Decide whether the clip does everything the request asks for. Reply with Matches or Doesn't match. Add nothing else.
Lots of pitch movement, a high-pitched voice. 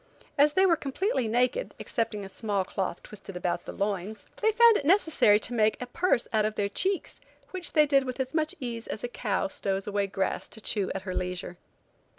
Matches